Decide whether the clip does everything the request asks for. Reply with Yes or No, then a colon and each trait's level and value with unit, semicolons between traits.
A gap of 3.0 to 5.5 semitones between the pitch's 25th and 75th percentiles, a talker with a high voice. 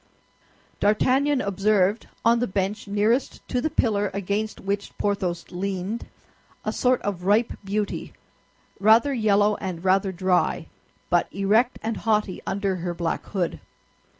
No: narrow, 2.5 semitones; high, 205 Hz